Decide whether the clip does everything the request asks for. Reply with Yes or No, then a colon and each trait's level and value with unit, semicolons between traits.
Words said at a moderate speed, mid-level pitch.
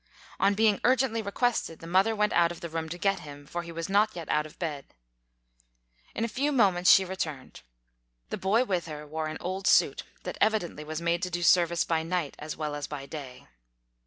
No: fast, 215 wpm; medium, 175 Hz